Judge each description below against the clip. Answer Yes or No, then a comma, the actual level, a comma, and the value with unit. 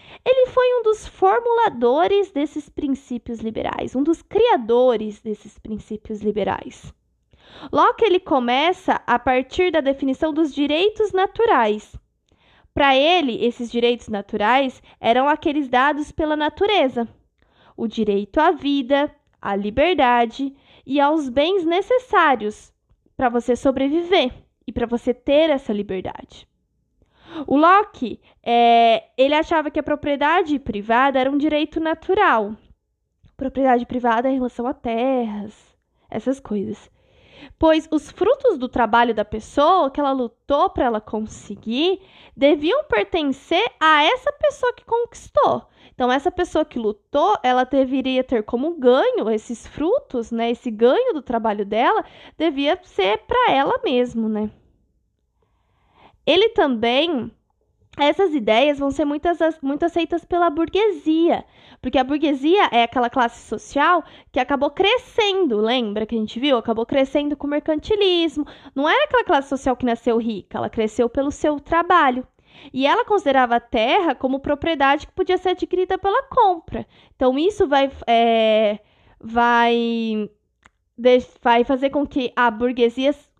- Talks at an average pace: Yes, average, 135 wpm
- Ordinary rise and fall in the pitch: No, wide, 5.8 semitones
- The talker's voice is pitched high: Yes, very high, 275 Hz